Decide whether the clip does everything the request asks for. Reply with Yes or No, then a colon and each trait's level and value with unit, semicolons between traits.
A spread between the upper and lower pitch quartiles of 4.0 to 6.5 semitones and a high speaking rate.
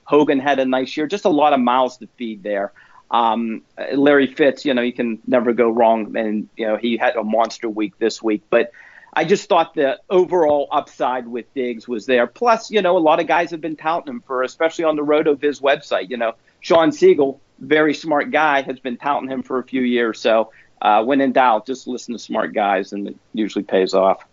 Yes: average, 4.9 semitones; fast, 225 wpm